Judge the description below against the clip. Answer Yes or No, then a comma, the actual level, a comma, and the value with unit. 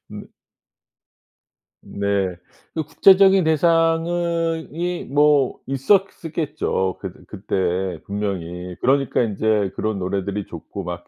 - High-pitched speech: No, low, 135 Hz